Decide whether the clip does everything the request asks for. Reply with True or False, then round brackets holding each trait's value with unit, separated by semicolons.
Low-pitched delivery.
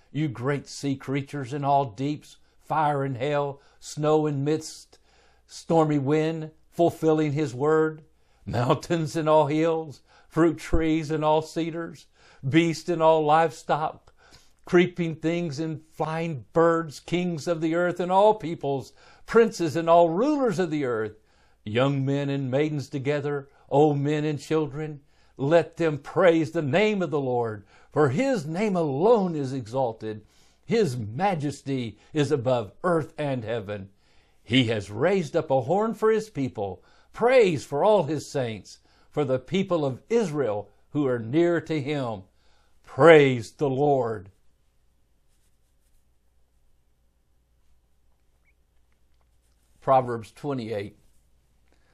False (145 Hz)